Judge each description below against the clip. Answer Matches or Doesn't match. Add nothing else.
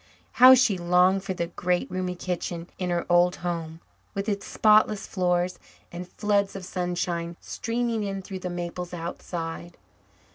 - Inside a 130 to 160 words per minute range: Matches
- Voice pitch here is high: Doesn't match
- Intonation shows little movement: Matches